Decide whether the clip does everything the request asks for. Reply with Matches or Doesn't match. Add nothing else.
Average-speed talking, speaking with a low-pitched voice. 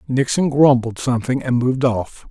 Matches